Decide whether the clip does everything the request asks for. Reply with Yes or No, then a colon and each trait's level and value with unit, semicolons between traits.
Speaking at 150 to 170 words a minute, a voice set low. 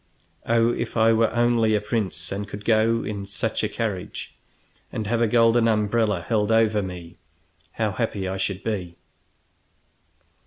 Yes: average, 155 wpm; low, 110 Hz